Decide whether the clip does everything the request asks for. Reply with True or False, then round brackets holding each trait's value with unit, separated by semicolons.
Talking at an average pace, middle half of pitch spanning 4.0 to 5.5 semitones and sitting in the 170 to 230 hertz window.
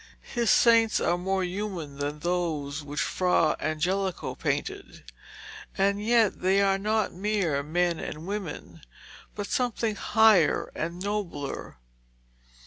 False (120 wpm; 4.6 semitones; 185 Hz)